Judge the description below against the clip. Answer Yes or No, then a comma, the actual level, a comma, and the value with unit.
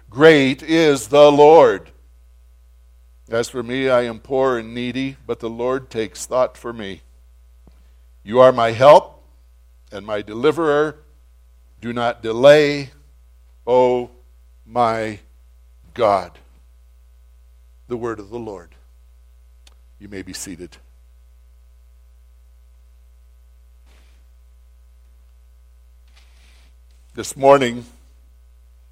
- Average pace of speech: No, slow, 90 wpm